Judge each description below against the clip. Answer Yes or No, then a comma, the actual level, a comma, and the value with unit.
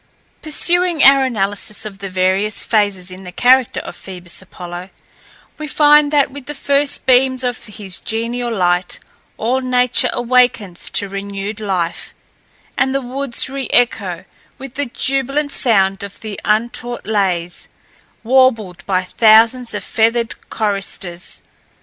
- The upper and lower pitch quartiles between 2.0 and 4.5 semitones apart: No, average, 5.1 semitones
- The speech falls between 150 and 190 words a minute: No, slow, 135 wpm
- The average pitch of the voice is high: Yes, high, 225 Hz